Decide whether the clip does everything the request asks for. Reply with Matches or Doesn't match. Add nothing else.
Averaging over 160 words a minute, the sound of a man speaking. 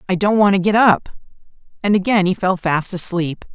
Doesn't match